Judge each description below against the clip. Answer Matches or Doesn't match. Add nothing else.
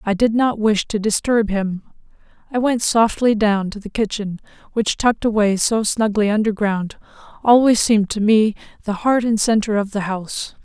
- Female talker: Matches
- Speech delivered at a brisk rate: Doesn't match